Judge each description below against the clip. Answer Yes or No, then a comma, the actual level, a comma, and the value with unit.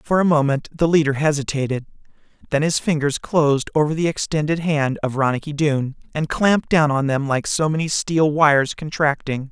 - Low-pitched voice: No, medium, 150 Hz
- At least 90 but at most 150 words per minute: No, average, 175 wpm